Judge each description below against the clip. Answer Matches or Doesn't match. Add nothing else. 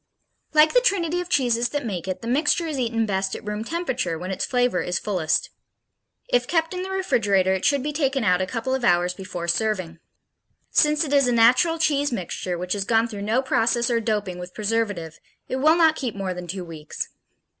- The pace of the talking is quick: Matches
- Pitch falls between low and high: Doesn't match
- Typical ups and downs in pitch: Doesn't match